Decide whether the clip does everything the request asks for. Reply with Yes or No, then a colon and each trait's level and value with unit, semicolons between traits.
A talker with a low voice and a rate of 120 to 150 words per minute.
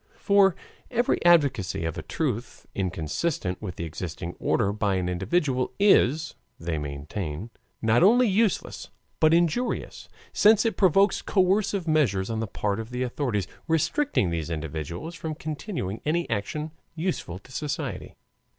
Yes: low, 125 Hz; average, 140 wpm